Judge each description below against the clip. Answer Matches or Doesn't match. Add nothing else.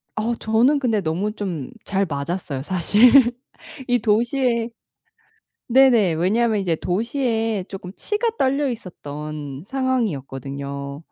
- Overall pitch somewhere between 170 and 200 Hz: Doesn't match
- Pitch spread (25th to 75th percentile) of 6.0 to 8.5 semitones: Matches